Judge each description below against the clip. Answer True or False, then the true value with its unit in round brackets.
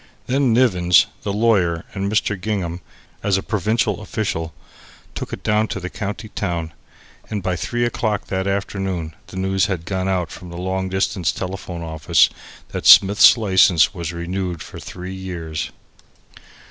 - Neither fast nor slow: True (155 wpm)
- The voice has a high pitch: False (95 Hz)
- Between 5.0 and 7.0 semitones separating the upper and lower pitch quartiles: False (3.0 semitones)